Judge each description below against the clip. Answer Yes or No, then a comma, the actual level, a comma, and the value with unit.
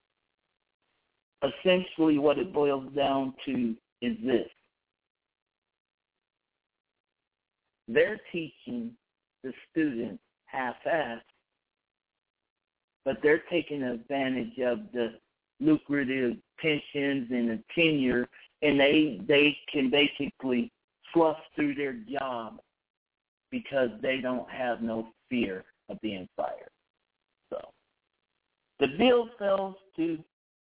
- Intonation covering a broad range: Yes, wide, 6.6 semitones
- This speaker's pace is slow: Yes, slow, 90 wpm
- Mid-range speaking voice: Yes, medium, 145 Hz